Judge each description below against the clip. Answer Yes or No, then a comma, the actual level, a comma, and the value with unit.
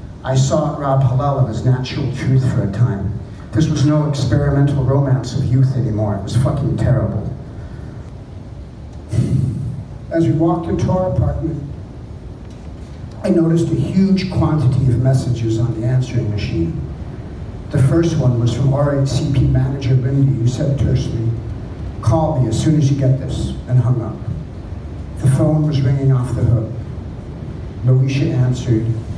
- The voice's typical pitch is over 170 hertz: No, low, 130 Hz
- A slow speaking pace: No, average, 145 wpm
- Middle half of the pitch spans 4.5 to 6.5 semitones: No, average, 3.5 semitones